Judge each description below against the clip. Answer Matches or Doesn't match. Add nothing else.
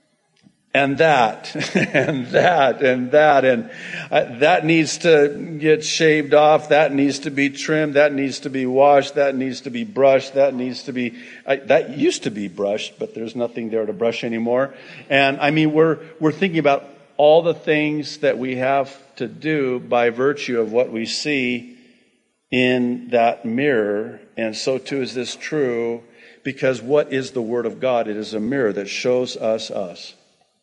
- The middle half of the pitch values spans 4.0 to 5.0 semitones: Doesn't match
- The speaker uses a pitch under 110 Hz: Doesn't match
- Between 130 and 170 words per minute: Doesn't match